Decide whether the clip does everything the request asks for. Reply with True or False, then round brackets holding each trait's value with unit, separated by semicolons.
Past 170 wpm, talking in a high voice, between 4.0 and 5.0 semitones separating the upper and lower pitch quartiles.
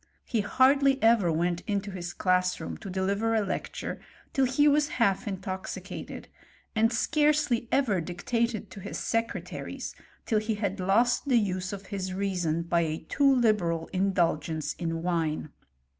False (155 wpm; 200 Hz; 4.6 semitones)